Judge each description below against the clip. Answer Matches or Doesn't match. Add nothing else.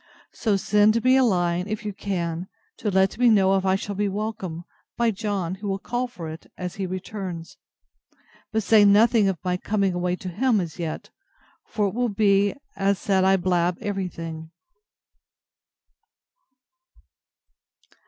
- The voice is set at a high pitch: Matches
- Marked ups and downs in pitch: Doesn't match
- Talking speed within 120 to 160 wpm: Matches